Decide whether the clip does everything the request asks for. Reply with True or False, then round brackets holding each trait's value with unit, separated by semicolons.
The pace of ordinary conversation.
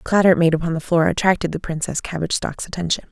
False (250 wpm)